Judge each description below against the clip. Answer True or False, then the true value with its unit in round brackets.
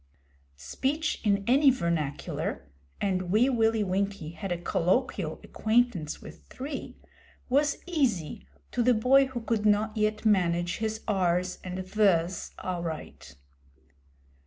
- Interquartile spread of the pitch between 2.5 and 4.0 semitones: False (5.5 semitones)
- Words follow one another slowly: True (120 wpm)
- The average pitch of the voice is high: True (205 Hz)